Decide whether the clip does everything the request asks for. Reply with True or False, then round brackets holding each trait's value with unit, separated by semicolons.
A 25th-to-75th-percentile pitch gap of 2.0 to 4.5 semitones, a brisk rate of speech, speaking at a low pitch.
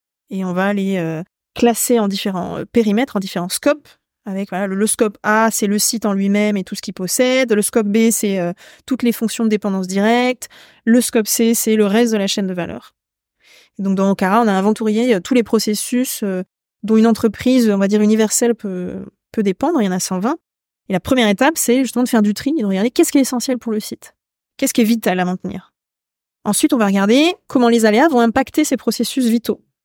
False (3.4 semitones; 235 wpm; 220 Hz)